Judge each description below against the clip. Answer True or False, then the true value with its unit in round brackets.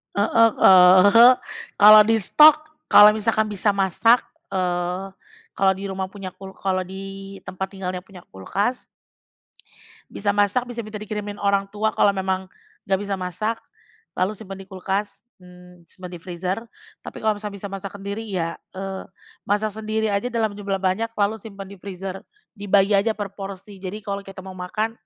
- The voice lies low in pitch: False (200 Hz)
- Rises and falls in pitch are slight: True (2.0 semitones)